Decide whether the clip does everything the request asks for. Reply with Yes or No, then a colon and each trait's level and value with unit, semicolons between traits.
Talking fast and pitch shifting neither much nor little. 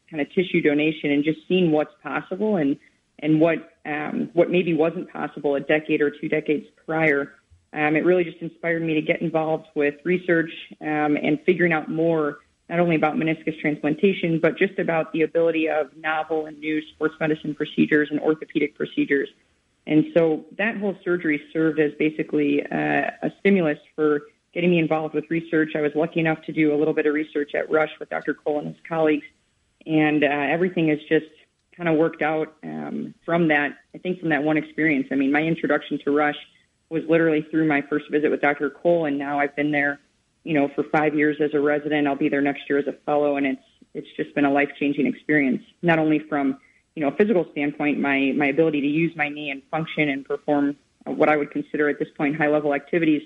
No: fast, 210 wpm; narrow, 1.6 semitones